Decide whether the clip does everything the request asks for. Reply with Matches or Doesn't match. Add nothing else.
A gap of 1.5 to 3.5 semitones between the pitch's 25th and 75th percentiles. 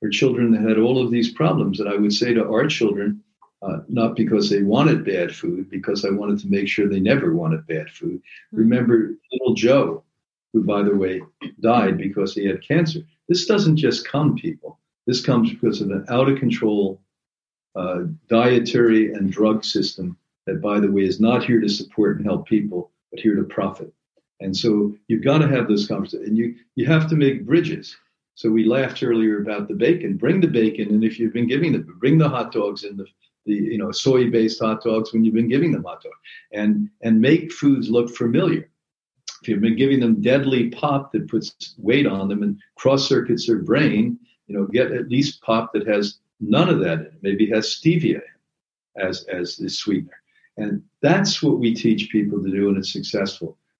Doesn't match